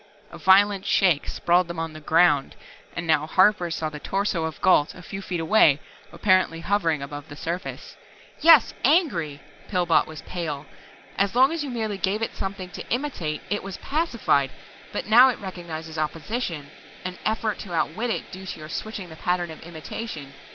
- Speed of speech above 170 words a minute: Yes, average, 180 wpm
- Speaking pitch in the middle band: Yes, medium, 180 Hz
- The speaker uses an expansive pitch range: No, average, 4.6 semitones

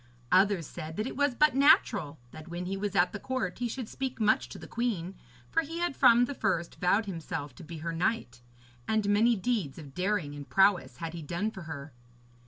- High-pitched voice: Yes, high, 195 Hz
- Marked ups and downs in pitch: Yes, wide, 5.9 semitones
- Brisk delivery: Yes, fast, 215 wpm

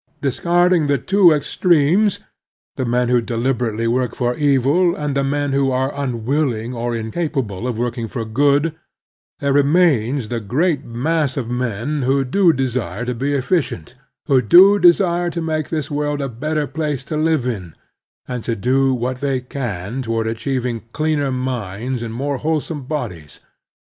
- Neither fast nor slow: Yes, average, 160 wpm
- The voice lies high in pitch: No, low, 135 Hz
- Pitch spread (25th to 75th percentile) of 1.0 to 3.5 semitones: No, average, 4.0 semitones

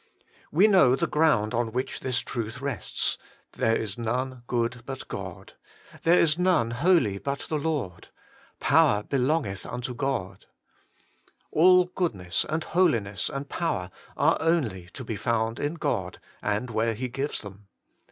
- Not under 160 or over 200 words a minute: Yes, average, 170 wpm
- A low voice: Yes, low, 125 Hz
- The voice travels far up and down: Yes, wide, 5.8 semitones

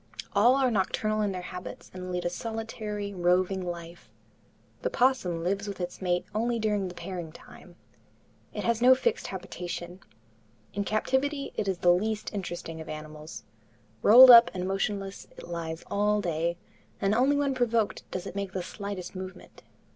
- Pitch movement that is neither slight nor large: Yes, average, 3.7 semitones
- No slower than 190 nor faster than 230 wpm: No, average, 165 wpm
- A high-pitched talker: Yes, high, 195 Hz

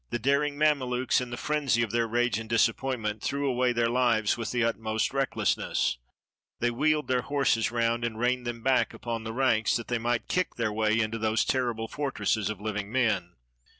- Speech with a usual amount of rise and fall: No, narrow, 2.3 semitones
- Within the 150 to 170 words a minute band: No, average, 190 wpm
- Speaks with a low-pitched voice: Yes, low, 120 Hz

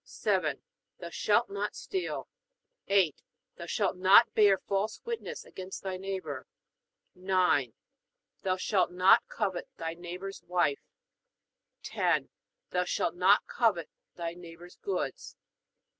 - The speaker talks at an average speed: No, slow, 115 wpm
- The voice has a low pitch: No, medium, 185 Hz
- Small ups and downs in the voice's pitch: Yes, narrow, 2.1 semitones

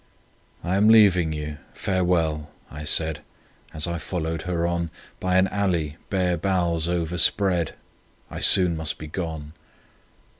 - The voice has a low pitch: Yes, very low, 85 Hz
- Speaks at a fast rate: No, slow, 135 wpm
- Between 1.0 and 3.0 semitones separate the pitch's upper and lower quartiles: Yes, narrow, 2.5 semitones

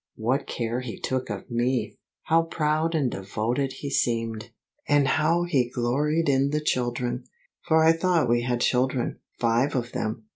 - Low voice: Yes, low, 130 Hz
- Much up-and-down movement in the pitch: No, average, 4.1 semitones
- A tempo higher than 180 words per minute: No, average, 160 wpm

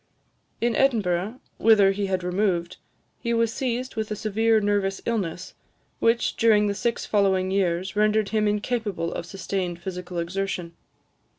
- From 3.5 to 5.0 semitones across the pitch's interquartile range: No, average, 3.1 semitones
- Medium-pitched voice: No, high, 200 Hz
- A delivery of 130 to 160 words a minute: Yes, average, 140 wpm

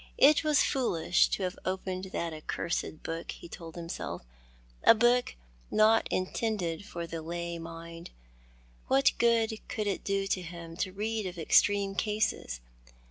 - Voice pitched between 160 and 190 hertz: Yes, medium, 185 Hz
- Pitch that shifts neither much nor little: Yes, average, 4.5 semitones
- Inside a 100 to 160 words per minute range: Yes, average, 140 wpm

